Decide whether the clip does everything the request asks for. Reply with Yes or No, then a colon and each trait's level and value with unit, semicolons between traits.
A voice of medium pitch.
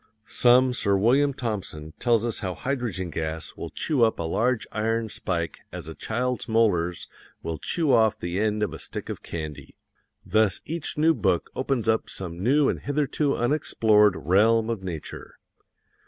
No: low, 110 Hz